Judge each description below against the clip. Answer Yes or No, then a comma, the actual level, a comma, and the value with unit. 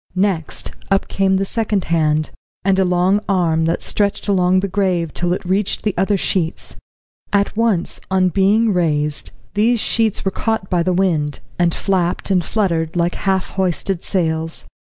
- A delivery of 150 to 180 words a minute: Yes, average, 165 wpm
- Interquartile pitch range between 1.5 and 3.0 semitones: Yes, narrow, 2.6 semitones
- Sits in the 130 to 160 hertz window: No, medium, 185 Hz